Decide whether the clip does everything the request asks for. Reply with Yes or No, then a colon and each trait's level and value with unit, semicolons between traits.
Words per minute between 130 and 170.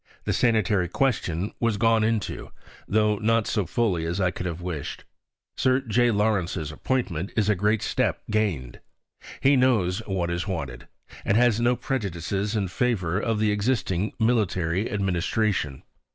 Yes: average, 150 wpm